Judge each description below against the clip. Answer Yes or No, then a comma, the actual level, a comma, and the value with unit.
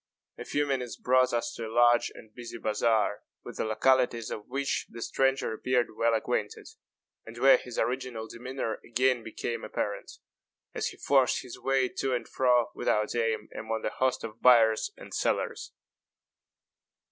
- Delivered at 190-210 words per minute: No, average, 160 wpm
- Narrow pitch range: Yes, narrow, 2.3 semitones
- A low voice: Yes, low, 120 Hz